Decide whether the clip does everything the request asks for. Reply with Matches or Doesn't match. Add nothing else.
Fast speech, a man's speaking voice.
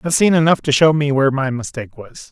Matches